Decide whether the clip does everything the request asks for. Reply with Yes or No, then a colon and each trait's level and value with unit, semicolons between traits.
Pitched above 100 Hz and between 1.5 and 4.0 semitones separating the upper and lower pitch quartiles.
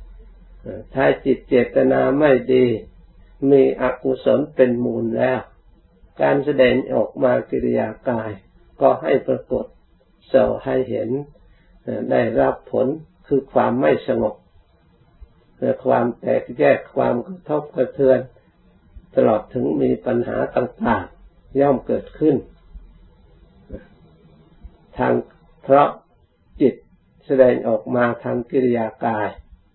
No: low, 125 Hz; wide, 5.6 semitones